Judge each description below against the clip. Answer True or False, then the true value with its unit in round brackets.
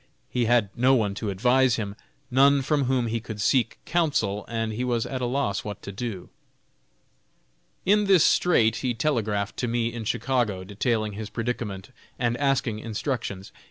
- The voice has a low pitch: True (115 Hz)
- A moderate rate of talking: True (165 wpm)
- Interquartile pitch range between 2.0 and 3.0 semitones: False (3.7 semitones)